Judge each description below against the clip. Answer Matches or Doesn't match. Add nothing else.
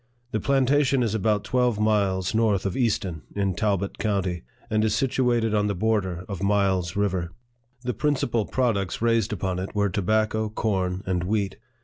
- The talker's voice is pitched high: Doesn't match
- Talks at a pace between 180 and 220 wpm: Doesn't match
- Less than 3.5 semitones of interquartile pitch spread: Matches